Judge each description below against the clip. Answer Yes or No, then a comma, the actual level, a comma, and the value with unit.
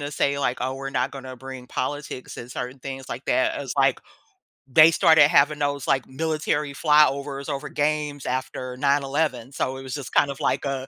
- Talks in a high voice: No, medium, 140 Hz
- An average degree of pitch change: No, narrow, 2.0 semitones